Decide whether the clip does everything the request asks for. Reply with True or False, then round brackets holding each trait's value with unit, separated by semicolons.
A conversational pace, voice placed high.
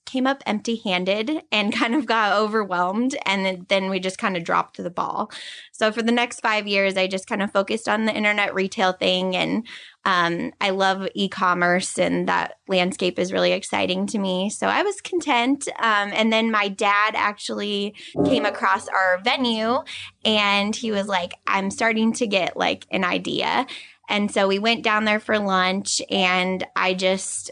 True (185 wpm; 205 Hz)